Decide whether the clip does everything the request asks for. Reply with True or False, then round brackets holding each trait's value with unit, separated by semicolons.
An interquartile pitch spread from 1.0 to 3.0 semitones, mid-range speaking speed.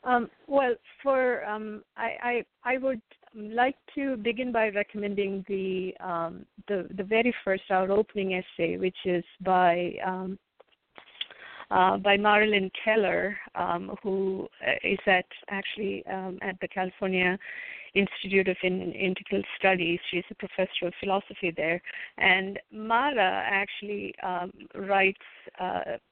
False (2.6 semitones; 125 wpm)